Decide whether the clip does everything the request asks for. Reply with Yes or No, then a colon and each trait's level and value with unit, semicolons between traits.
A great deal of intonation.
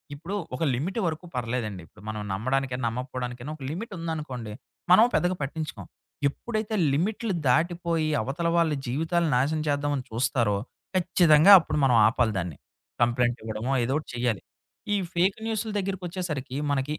Yes: wide, 5.7 semitones